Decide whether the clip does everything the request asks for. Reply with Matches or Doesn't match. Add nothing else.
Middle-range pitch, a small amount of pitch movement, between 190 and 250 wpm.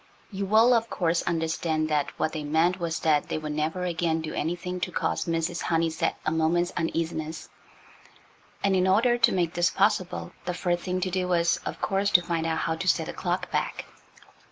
Matches